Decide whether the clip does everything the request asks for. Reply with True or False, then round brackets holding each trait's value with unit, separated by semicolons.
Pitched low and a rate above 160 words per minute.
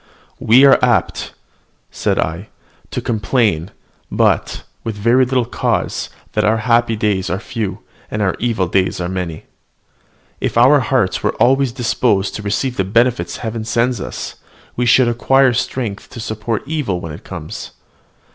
False (115 Hz; 150 wpm)